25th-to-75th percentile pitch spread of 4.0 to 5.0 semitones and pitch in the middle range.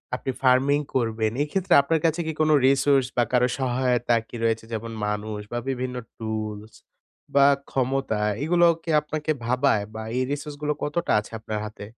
No: average, 4.6 semitones; low, 130 Hz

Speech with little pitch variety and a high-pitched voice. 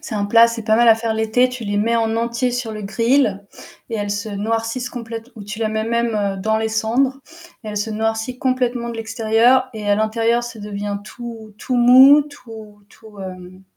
Yes: narrow, 2.0 semitones; high, 225 Hz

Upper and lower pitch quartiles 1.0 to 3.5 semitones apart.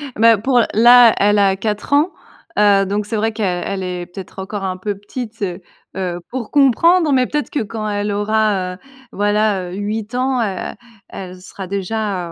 Yes: average, 2.9 semitones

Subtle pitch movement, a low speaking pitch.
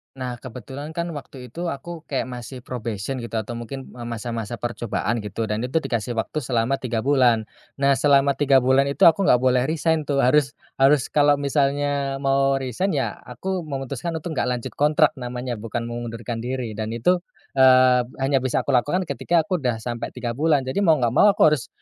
No: average, 3.3 semitones; low, 130 Hz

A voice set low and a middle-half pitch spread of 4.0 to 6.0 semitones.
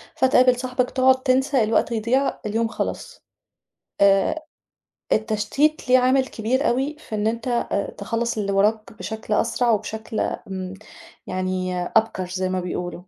No: high, 225 Hz; average, 4.3 semitones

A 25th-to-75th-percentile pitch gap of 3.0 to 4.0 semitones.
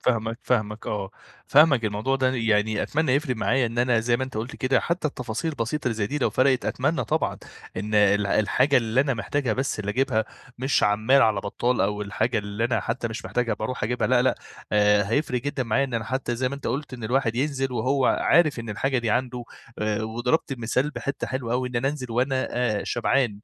Yes: average, 3.3 semitones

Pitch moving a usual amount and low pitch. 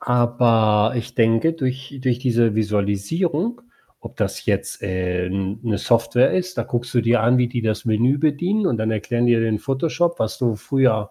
Yes: average, 3.3 semitones; low, 120 Hz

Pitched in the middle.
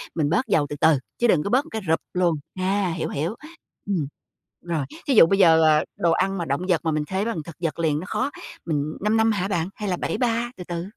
Yes: medium, 175 Hz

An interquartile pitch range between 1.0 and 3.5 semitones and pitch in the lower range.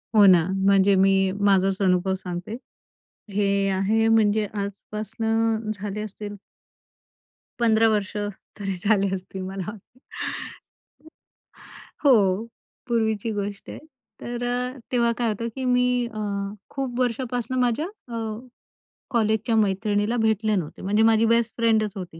No: average, 2.8 semitones; high, 215 Hz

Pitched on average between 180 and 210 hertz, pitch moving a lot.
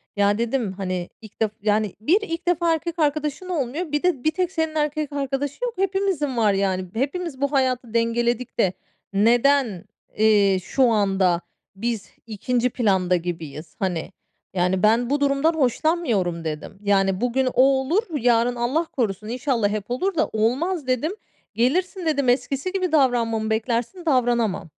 No: high, 245 Hz; wide, 6.2 semitones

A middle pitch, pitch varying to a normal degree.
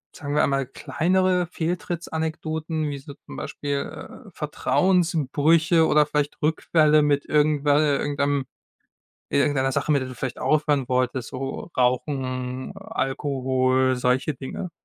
Yes: medium, 145 Hz; average, 3.1 semitones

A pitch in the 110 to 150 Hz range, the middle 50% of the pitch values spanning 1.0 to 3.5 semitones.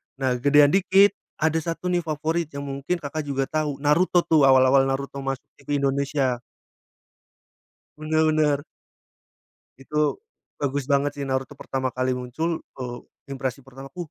Yes: medium, 140 Hz; narrow, 2.6 semitones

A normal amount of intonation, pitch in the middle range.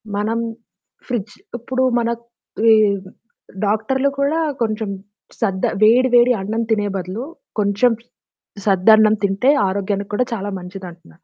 No: average, 3.0 semitones; high, 215 Hz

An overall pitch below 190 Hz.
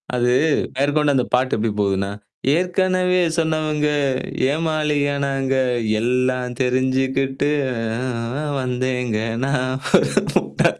Yes: low, 135 Hz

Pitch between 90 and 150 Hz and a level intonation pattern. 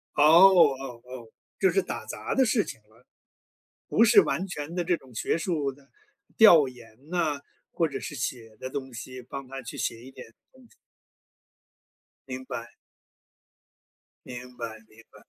No: medium, 140 Hz; wide, 5.6 semitones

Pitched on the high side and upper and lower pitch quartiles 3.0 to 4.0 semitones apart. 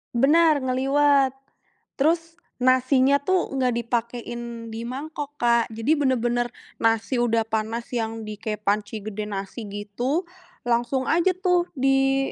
Yes: high, 245 Hz; average, 3.6 semitones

